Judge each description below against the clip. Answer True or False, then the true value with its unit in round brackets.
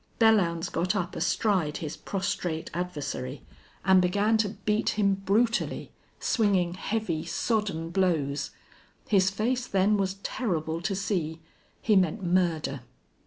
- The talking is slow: True (120 wpm)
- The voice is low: False (190 Hz)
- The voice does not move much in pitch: False (3.8 semitones)